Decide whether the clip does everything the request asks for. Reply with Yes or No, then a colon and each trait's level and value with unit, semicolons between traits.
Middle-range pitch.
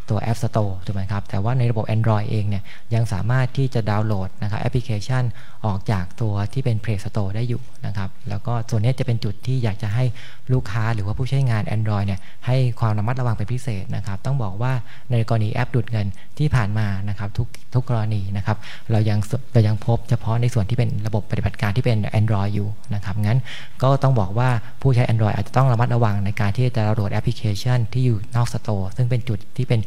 No: low, 115 Hz